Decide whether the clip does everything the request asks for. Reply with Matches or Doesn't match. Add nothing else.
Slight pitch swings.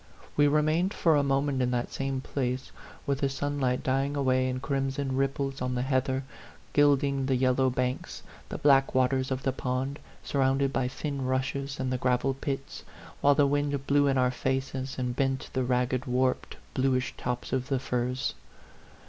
Matches